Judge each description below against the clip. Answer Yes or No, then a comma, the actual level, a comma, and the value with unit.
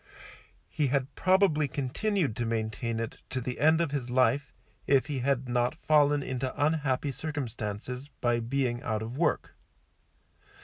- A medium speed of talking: Yes, average, 145 wpm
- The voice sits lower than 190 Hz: Yes, low, 135 Hz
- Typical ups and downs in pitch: Yes, average, 3.4 semitones